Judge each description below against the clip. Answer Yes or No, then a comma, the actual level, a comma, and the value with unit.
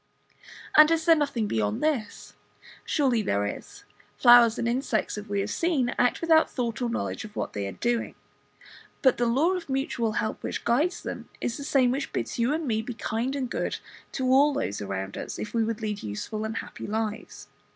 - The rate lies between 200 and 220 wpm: Yes, fast, 205 wpm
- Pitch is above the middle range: Yes, high, 240 Hz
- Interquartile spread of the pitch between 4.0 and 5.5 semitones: Yes, average, 4.6 semitones